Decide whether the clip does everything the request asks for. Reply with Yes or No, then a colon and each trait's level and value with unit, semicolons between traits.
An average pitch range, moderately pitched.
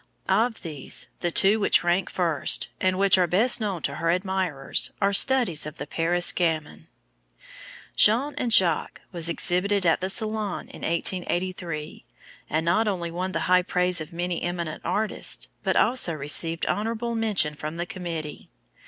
Yes: average, 3.2 semitones; medium, 180 Hz